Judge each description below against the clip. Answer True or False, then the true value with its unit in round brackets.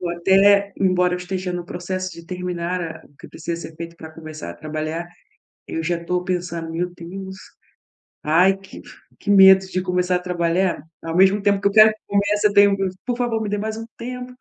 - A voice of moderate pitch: True (180 Hz)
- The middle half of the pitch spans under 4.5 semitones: True (2.7 semitones)